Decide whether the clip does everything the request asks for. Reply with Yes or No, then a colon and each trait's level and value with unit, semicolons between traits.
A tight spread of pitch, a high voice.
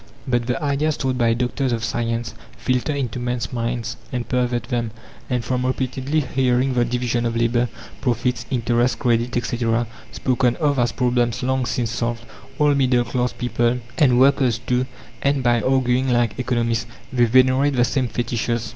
No: narrow, 1.6 semitones; low, 125 Hz